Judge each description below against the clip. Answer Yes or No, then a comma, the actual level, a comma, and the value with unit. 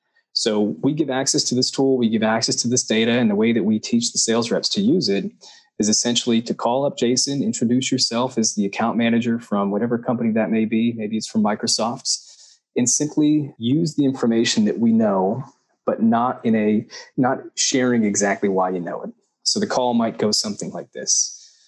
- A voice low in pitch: Yes, low, 120 Hz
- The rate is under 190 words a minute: No, fast, 205 wpm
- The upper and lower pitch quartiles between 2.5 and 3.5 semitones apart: No, average, 4.1 semitones